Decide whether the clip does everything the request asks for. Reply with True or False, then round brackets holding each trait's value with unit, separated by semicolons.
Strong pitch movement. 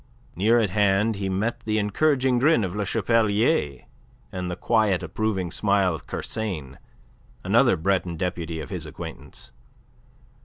False (3.6 semitones)